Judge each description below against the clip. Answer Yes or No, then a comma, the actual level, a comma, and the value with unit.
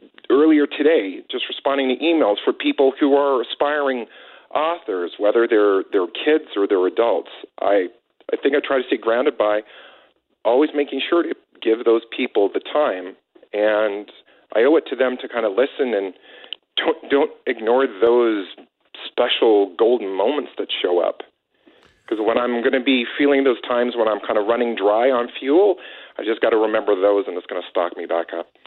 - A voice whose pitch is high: No, medium, 140 Hz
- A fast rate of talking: No, average, 185 wpm